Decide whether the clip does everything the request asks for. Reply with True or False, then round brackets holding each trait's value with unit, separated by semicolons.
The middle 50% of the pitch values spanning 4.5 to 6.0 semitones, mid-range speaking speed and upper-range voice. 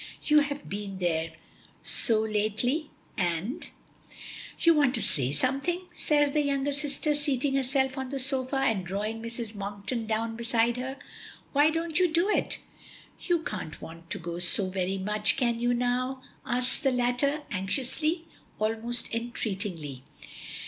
True (5.3 semitones; 150 wpm; 245 Hz)